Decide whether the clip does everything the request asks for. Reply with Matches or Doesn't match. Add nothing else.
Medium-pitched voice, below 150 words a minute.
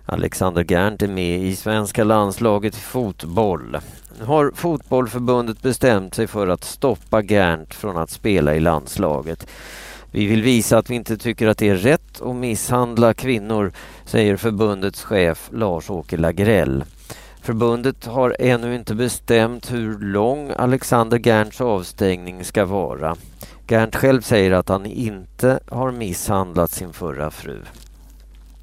Doesn't match